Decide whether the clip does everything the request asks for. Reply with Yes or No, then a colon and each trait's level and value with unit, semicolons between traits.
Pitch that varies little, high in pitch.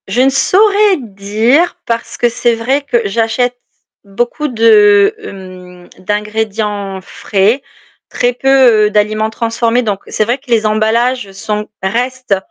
No: average, 3.2 semitones; high, 225 Hz